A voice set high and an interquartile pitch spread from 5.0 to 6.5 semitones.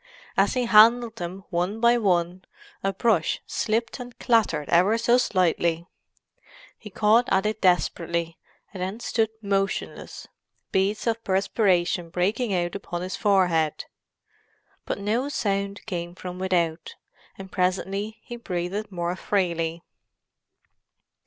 No: high, 195 Hz; average, 3.7 semitones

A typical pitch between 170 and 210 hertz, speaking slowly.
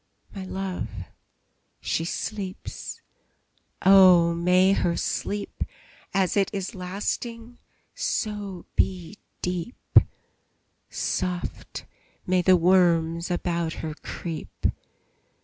Yes: medium, 185 Hz; slow, 85 wpm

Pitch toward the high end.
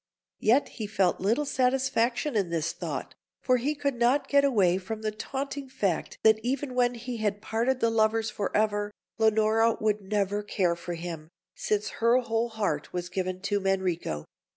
Yes: high, 220 Hz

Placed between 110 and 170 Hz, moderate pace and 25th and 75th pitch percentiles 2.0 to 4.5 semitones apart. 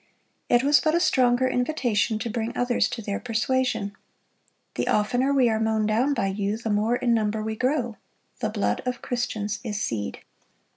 No: high, 230 Hz; average, 180 wpm; average, 2.8 semitones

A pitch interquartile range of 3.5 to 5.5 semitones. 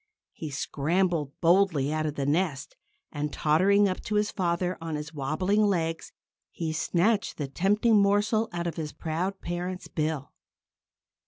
Yes: average, 4.2 semitones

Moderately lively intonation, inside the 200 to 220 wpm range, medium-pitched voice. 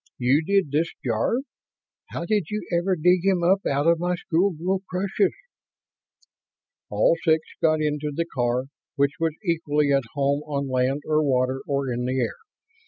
No: average, 4.3 semitones; average, 165 wpm; medium, 155 Hz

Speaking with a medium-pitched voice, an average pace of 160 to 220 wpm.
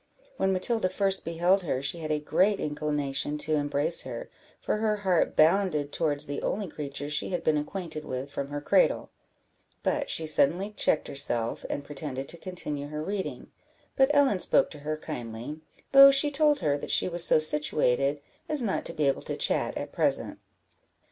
Yes: medium, 155 Hz; average, 180 wpm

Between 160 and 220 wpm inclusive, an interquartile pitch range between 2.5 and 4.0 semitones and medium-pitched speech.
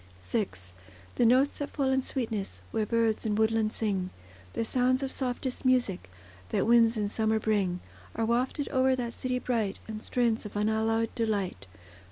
No: average, 165 wpm; average, 2.8 semitones; high, 225 Hz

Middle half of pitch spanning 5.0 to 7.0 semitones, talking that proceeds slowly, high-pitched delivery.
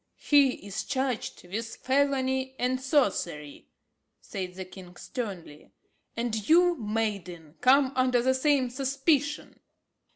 Yes: average, 5.3 semitones; slow, 110 wpm; very high, 250 Hz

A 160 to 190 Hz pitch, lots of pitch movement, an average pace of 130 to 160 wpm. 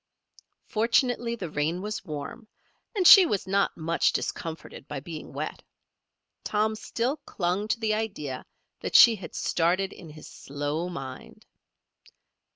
Yes: medium, 185 Hz; wide, 5.8 semitones; slow, 135 wpm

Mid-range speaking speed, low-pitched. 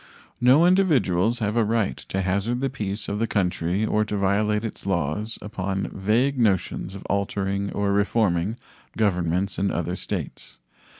Yes: average, 155 wpm; low, 100 Hz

